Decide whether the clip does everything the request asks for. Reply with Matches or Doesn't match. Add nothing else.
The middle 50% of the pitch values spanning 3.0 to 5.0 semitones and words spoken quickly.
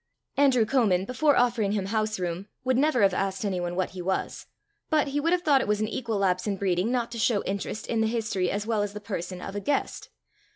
Matches